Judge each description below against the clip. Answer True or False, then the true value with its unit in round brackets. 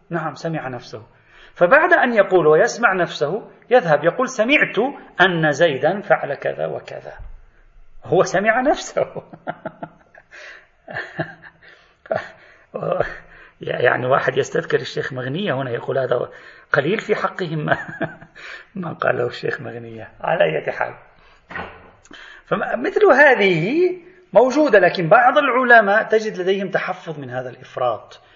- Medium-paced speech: True (105 wpm)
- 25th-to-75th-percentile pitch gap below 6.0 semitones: False (8.4 semitones)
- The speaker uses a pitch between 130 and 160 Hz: False (190 Hz)